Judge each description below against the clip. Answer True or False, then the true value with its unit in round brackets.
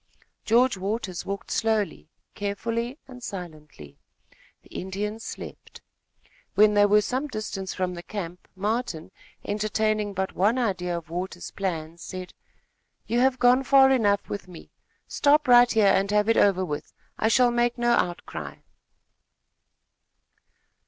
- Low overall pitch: False (205 Hz)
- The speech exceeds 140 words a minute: False (135 wpm)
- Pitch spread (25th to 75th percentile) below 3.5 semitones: False (4.3 semitones)